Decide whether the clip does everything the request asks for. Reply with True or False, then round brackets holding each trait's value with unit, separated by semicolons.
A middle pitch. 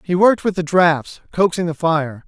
True (170 Hz)